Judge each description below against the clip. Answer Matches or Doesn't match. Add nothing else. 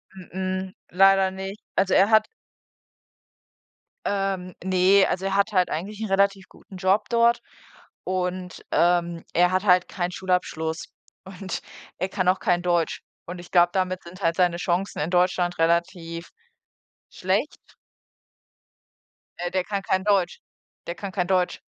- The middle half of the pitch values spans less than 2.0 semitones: Matches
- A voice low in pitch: Doesn't match